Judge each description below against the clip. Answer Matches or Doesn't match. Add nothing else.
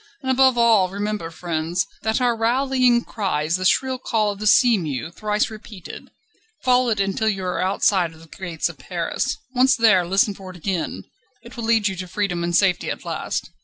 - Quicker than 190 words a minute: Matches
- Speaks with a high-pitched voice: Matches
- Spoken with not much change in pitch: Doesn't match